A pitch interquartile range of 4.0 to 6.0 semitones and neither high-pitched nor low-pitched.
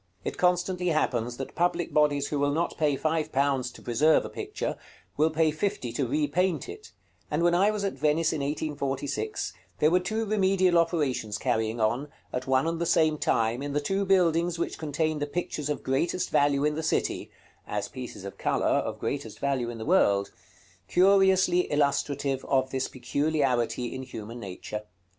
Yes: average, 4.6 semitones; medium, 150 Hz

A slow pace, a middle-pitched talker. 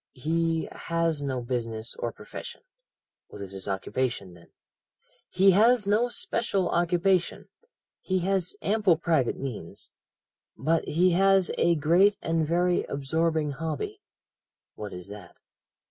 Yes: slow, 125 wpm; medium, 165 Hz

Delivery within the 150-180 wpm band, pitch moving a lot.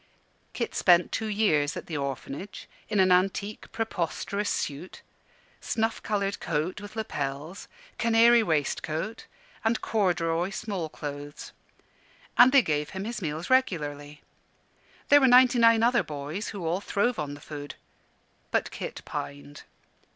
No: slow, 135 wpm; wide, 6.8 semitones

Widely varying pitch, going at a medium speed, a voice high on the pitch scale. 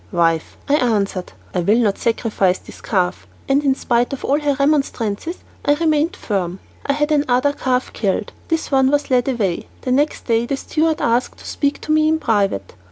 Yes: wide, 5.9 semitones; average, 190 wpm; very high, 255 Hz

